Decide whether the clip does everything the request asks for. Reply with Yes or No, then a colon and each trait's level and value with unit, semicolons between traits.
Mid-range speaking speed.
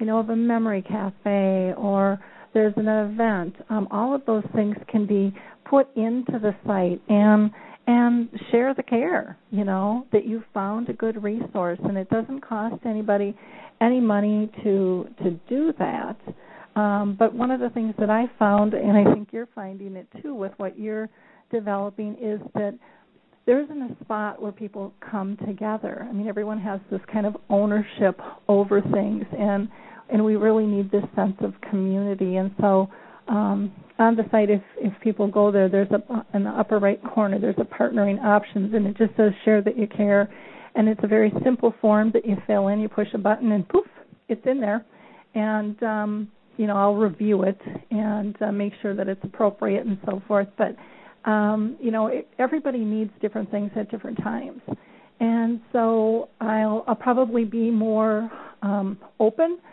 Yes: average, 180 wpm